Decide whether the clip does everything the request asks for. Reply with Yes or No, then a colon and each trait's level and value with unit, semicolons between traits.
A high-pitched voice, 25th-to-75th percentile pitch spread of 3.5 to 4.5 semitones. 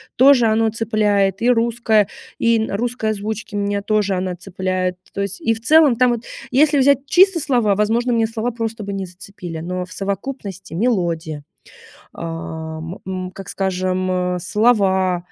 Yes: high, 210 Hz; average, 3.8 semitones